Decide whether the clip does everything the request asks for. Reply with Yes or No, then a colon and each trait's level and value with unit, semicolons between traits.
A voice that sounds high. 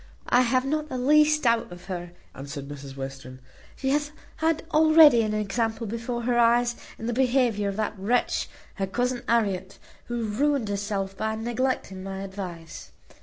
Yes: high, 225 Hz